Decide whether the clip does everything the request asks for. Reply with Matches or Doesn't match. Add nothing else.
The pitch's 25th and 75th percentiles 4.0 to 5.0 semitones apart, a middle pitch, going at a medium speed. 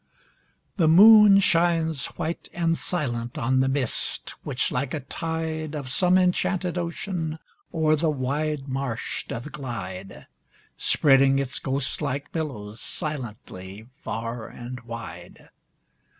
Doesn't match